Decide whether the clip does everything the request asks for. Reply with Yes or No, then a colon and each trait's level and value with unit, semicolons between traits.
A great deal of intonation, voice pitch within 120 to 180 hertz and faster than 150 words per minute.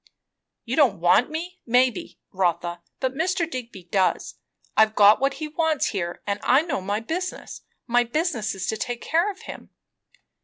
No: wide, 7.6 semitones; high, 245 Hz; average, 165 wpm